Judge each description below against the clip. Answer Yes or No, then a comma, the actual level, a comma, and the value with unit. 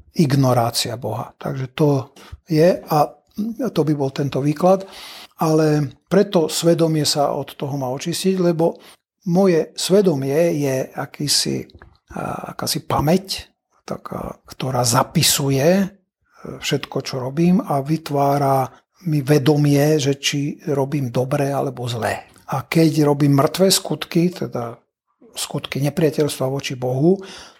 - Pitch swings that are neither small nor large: Yes, average, 3.8 semitones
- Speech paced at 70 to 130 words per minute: Yes, average, 115 wpm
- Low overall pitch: No, medium, 150 Hz